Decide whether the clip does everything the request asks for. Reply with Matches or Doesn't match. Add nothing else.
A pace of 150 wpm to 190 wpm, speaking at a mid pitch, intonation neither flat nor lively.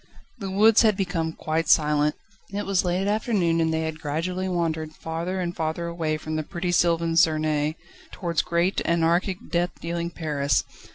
Doesn't match